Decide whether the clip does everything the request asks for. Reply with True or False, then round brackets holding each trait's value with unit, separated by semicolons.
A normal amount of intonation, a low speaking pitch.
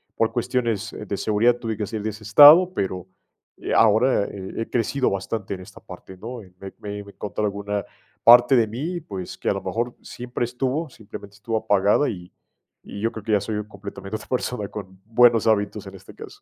True (3.1 semitones; 110 Hz)